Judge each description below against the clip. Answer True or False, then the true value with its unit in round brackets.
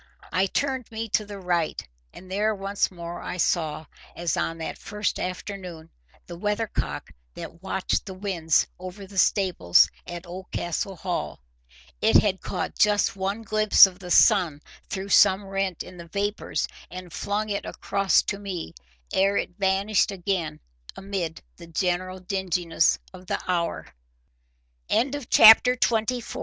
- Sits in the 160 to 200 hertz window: True (190 Hz)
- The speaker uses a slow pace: True (130 wpm)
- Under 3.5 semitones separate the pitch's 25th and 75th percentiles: True (2.5 semitones)